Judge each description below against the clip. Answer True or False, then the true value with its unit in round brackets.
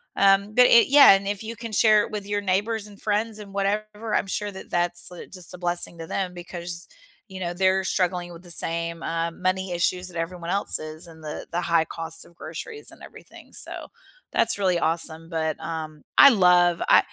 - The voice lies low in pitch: False (180 Hz)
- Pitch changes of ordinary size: True (3.2 semitones)